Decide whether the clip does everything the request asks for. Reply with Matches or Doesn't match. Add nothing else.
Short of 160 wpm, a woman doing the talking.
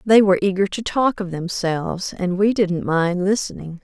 Doesn't match